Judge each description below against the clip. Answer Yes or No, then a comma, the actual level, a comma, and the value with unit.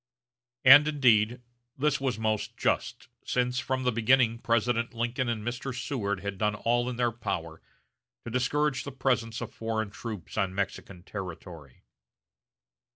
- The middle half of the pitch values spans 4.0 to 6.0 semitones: No, average, 3.1 semitones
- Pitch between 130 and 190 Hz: No, low, 115 Hz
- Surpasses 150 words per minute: No, average, 145 wpm